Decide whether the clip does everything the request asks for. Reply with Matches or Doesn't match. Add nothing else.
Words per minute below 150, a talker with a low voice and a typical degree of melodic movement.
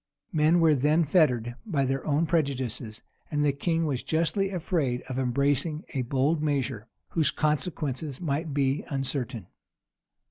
Doesn't match